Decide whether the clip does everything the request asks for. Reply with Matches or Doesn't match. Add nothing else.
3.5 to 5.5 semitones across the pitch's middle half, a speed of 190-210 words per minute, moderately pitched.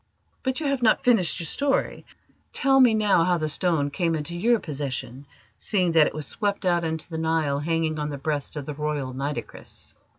Matches